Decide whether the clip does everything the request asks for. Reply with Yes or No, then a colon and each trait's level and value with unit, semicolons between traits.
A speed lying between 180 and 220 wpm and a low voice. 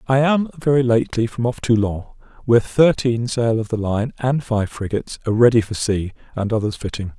Yes: average, 190 wpm; low, 115 Hz